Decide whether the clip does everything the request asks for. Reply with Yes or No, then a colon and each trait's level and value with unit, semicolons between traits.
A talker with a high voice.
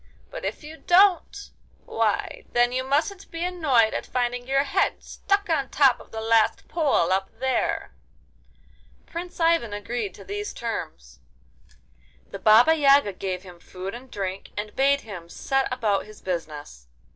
Yes: high, 245 Hz